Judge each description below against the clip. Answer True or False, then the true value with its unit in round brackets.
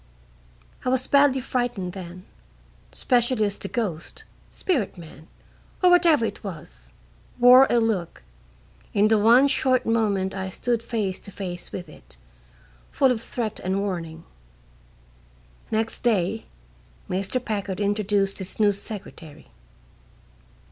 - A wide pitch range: False (4.4 semitones)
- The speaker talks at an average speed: False (125 wpm)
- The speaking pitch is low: False (210 Hz)